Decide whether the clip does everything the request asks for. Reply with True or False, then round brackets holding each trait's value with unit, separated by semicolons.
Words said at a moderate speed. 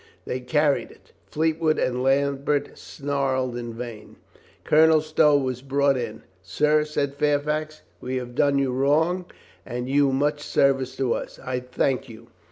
True (155 wpm)